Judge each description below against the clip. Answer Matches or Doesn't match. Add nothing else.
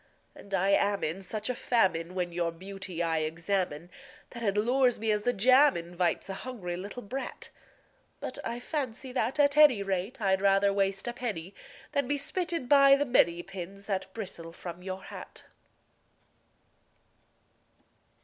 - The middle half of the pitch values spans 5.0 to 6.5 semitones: Matches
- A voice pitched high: Matches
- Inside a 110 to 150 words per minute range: Doesn't match